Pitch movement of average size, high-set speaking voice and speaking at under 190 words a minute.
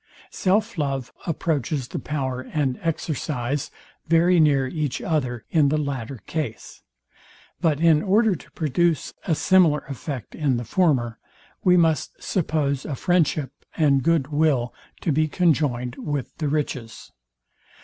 No: average, 3.7 semitones; medium, 150 Hz; slow, 135 wpm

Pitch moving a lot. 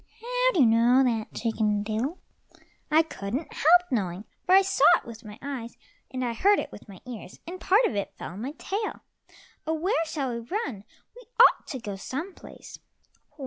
Yes: wide, 8.2 semitones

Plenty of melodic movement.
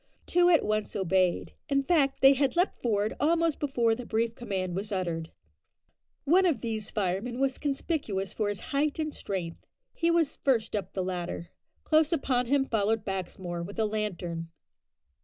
Yes: wide, 6.6 semitones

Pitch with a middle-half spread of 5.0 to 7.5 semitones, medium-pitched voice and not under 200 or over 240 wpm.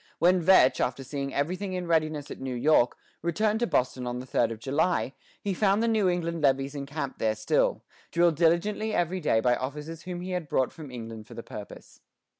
Yes: wide, 5.4 semitones; medium, 155 Hz; fast, 205 wpm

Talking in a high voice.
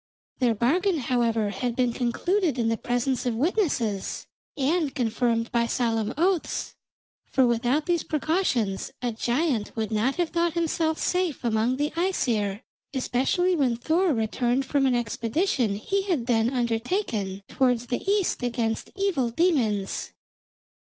Yes: very high, 250 Hz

